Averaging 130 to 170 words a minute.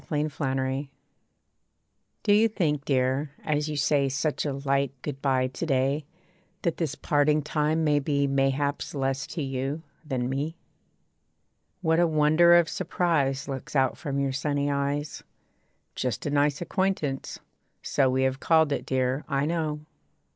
Yes: average, 155 wpm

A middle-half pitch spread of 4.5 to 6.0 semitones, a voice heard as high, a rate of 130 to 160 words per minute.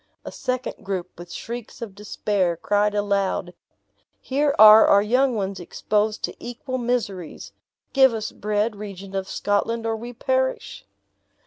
No: average, 3.4 semitones; high, 210 Hz; average, 140 wpm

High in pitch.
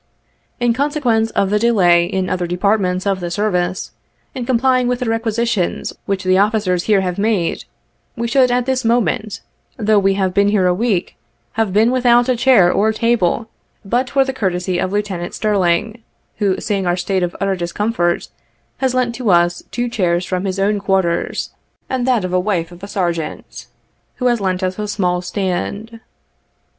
Yes: high, 205 Hz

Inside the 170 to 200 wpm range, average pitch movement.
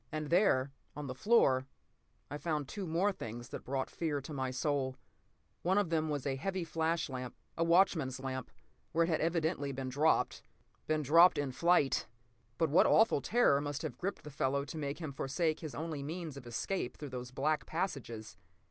Yes: average, 185 wpm; average, 3.9 semitones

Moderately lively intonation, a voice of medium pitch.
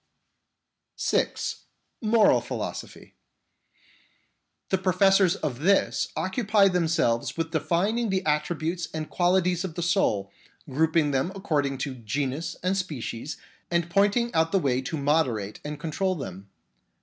Yes: average, 4.7 semitones; medium, 165 Hz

